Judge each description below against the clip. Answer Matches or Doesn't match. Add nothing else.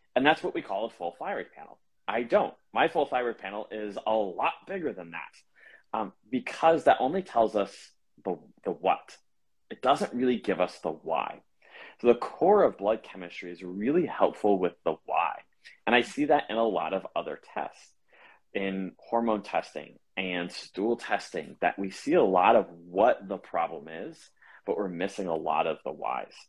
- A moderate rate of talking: Matches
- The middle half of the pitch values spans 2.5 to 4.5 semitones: Matches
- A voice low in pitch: Matches